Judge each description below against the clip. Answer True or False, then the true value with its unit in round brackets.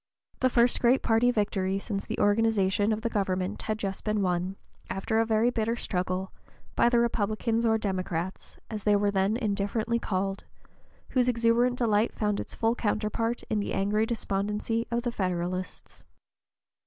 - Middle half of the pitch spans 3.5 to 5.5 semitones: False (2.9 semitones)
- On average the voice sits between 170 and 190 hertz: False (215 Hz)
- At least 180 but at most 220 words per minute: False (160 wpm)